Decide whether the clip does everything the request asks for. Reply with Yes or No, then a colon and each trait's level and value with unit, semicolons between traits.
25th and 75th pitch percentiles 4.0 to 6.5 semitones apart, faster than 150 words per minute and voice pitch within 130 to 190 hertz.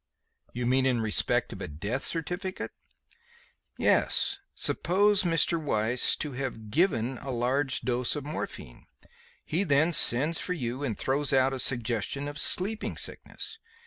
No: average, 5.2 semitones; average, 145 wpm; low, 135 Hz